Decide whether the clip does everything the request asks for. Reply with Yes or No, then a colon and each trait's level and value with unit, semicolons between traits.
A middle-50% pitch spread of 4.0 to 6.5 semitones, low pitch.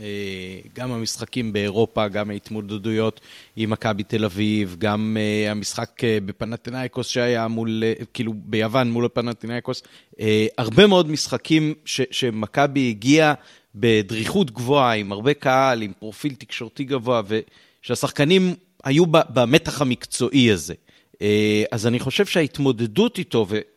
No: average, 3.6 semitones; low, 120 Hz